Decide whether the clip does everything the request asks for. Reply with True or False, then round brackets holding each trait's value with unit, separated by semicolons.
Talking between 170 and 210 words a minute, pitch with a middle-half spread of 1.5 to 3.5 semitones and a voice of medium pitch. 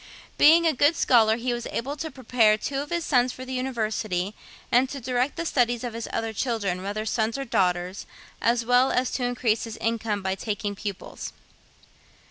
False (190 wpm; 3.1 semitones; 235 Hz)